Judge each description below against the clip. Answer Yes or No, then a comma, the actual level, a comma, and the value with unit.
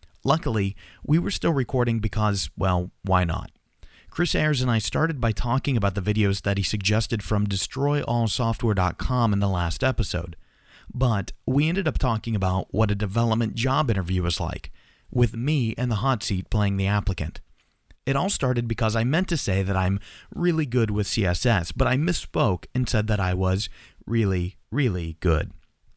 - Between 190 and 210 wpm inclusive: No, average, 175 wpm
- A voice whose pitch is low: Yes, low, 110 Hz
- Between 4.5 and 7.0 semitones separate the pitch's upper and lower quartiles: Yes, average, 5.1 semitones